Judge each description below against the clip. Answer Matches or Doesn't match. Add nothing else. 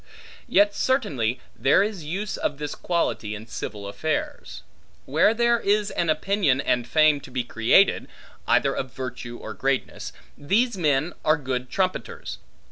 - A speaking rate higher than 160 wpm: Doesn't match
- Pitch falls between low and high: Matches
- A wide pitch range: Matches